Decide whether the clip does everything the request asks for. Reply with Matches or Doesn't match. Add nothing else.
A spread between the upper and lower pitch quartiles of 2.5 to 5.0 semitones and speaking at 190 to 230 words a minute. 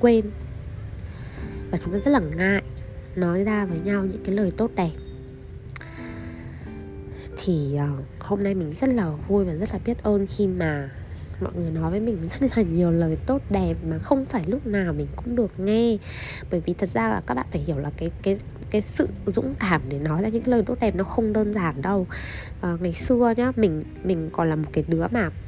Doesn't match